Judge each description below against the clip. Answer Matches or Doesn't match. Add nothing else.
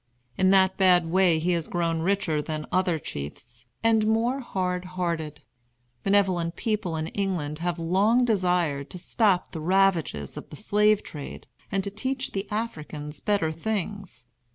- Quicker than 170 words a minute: Doesn't match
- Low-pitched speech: Doesn't match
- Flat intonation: Doesn't match